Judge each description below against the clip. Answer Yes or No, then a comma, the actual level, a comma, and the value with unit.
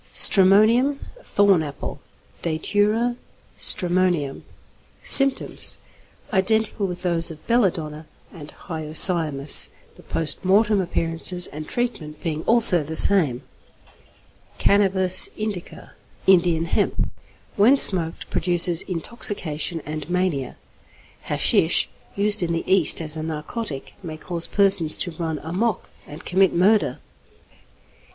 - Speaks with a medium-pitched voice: Yes, medium, 175 Hz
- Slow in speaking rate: Yes, slow, 110 wpm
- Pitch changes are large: No, average, 4.0 semitones